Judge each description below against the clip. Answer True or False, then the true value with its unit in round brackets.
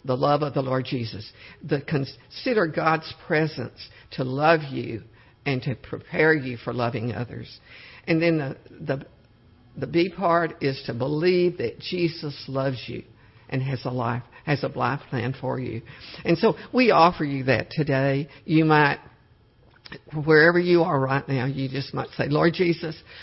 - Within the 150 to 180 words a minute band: True (165 wpm)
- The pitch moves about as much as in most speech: True (4.3 semitones)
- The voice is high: False (135 Hz)